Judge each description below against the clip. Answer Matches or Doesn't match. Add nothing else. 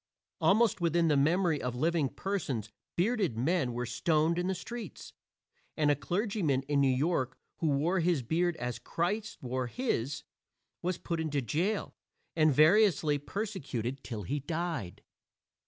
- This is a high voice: Doesn't match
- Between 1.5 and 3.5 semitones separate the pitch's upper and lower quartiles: Doesn't match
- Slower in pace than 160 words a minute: Matches